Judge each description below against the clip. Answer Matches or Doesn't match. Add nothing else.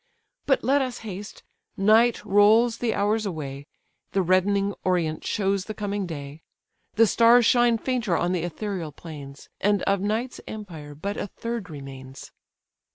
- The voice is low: Doesn't match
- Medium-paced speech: Matches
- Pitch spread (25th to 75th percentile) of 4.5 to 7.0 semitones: Matches